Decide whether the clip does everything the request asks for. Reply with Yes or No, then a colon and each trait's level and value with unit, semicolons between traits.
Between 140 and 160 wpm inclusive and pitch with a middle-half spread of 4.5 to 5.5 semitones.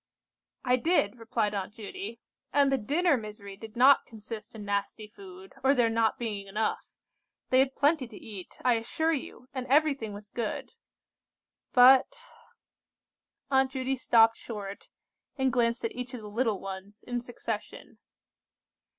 No: average, 150 wpm; average, 3.9 semitones